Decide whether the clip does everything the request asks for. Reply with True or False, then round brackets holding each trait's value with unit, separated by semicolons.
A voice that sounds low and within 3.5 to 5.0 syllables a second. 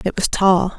False (190 Hz; 4.4 syllables/s)